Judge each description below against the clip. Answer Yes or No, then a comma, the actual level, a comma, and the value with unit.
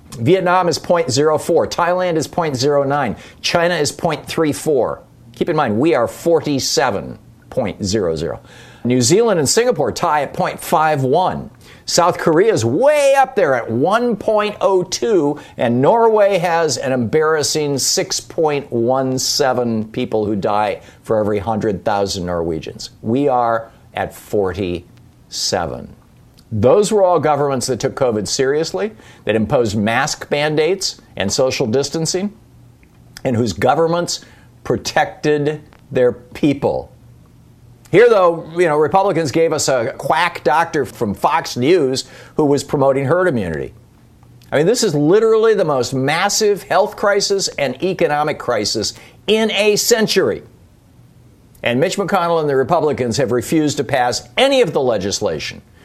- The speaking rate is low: Yes, slow, 125 wpm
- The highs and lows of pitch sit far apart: Yes, wide, 6.9 semitones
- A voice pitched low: No, medium, 150 Hz